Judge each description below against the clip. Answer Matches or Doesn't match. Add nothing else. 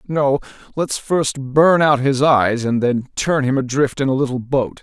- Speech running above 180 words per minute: Matches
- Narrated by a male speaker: Matches